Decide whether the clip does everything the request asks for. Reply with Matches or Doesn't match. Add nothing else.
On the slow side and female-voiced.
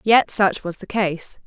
Doesn't match